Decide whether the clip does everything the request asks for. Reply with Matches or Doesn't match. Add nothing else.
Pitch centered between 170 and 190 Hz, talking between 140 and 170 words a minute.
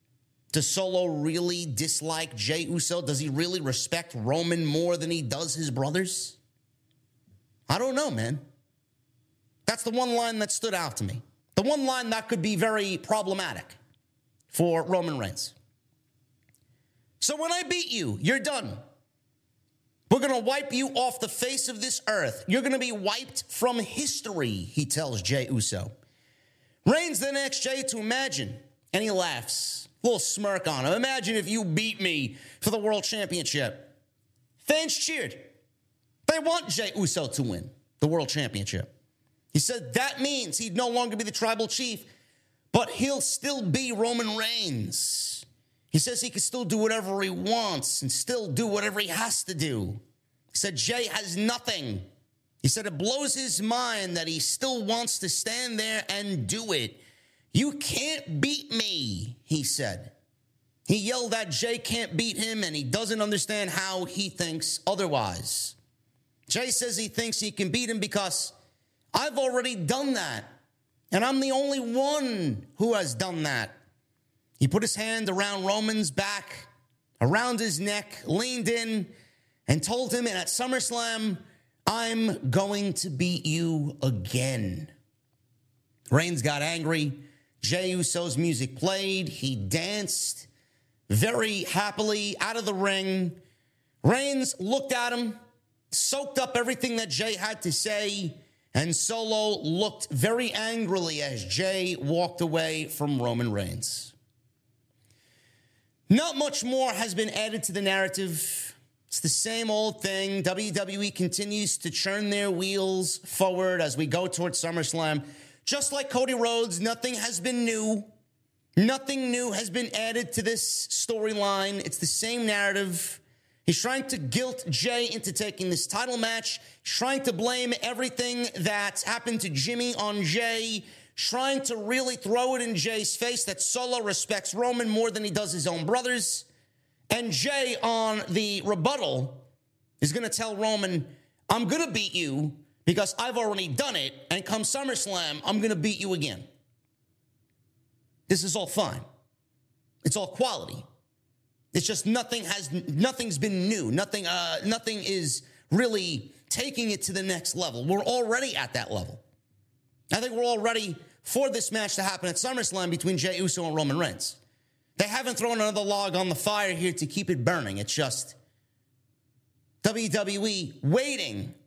Matches